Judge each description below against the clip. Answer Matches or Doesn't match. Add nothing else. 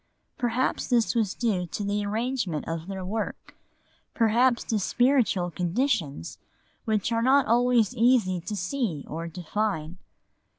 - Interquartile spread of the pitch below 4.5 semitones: Doesn't match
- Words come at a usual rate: Doesn't match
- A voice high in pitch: Matches